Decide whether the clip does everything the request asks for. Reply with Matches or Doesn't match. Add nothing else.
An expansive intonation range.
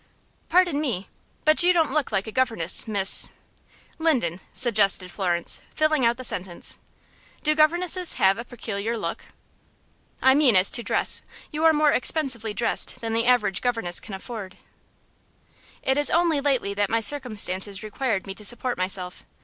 Matches